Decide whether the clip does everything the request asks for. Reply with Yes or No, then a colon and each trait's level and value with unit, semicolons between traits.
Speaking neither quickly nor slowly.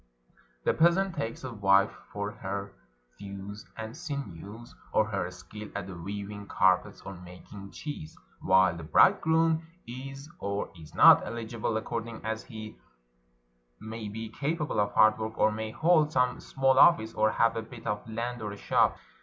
Yes: average, 160 wpm